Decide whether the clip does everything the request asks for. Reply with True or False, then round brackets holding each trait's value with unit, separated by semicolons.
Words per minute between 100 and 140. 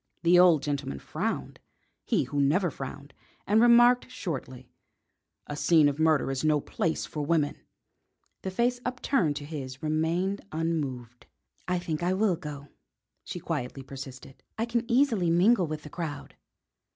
False (150 wpm)